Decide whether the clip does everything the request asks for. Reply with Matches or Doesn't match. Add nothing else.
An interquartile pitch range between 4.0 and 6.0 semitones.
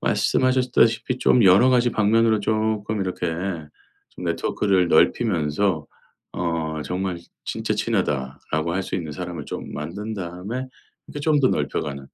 Matches